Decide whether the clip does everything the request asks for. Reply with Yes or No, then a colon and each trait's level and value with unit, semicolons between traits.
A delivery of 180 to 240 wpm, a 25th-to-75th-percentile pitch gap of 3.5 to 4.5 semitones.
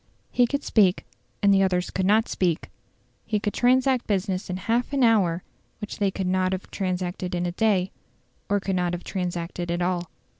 No: average, 190 wpm; average, 2.9 semitones